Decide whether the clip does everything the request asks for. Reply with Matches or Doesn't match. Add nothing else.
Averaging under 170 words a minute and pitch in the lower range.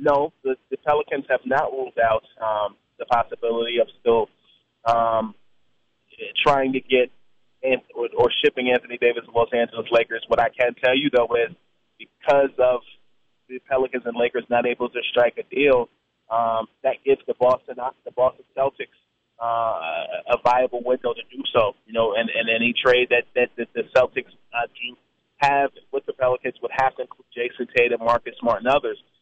Doesn't match